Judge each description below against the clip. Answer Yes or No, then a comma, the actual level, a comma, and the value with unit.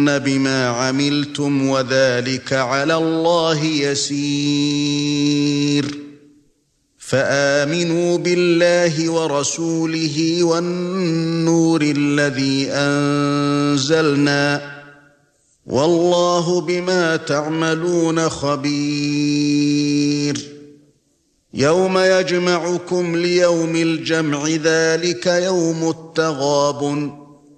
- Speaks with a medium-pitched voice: Yes, medium, 145 Hz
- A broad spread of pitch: No, narrow, 2.4 semitones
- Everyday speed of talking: No, slow, 50 wpm